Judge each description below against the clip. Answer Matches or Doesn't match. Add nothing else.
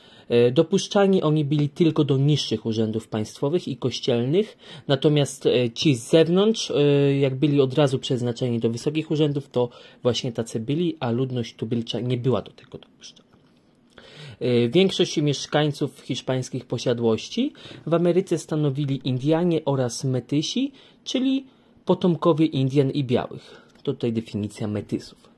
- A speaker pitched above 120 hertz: Matches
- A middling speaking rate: Matches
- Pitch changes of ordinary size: Matches